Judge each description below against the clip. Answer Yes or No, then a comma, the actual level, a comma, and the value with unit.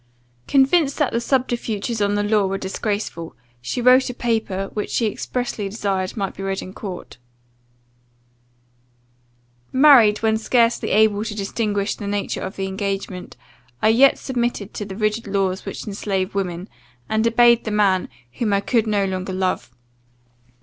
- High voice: Yes, high, 210 Hz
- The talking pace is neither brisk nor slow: Yes, average, 155 wpm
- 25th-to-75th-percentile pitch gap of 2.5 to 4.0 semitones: Yes, average, 3.1 semitones